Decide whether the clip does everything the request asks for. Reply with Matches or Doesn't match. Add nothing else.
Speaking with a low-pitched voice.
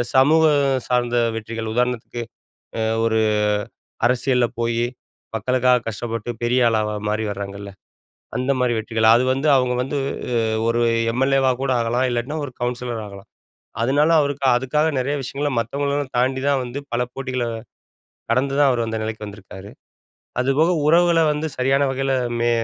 Matches